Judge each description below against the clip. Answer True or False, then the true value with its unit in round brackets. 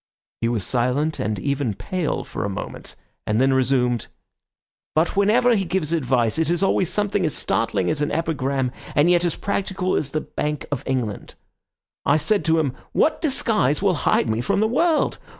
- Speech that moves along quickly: False (185 wpm)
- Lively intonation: True (6.5 semitones)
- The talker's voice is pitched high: False (150 Hz)